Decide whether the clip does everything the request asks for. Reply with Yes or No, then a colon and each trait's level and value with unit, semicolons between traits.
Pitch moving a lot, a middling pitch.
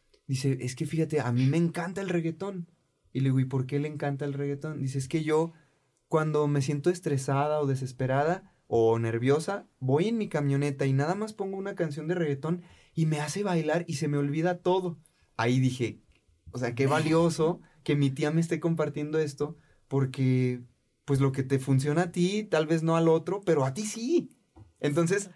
No: average, 3.6 semitones; medium, 150 Hz